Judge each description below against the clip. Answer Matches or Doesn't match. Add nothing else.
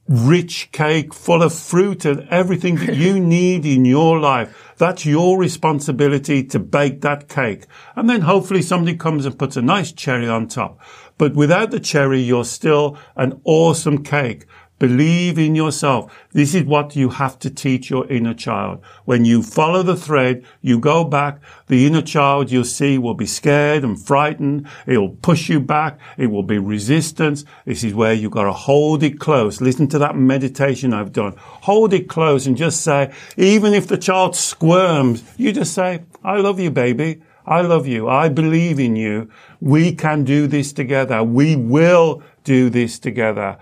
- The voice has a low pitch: Doesn't match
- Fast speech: Doesn't match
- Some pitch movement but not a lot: Matches